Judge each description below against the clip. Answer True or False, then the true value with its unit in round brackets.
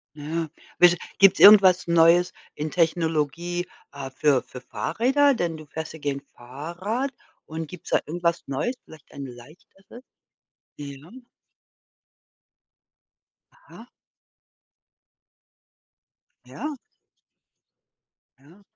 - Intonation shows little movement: False (3.8 semitones)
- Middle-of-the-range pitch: True (165 Hz)